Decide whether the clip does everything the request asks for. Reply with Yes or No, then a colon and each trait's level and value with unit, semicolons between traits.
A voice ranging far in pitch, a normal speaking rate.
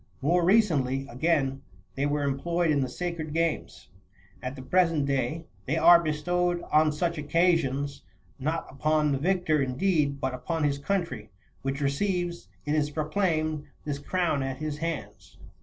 No: average, 3.5 semitones; average, 155 wpm